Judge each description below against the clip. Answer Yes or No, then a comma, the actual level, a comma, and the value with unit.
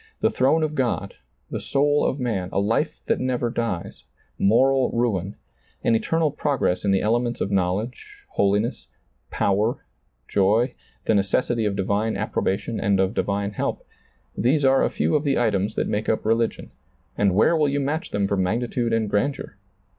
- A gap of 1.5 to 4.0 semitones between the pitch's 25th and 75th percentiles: No, average, 4.6 semitones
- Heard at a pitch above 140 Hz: No, low, 115 Hz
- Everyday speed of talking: Yes, average, 170 wpm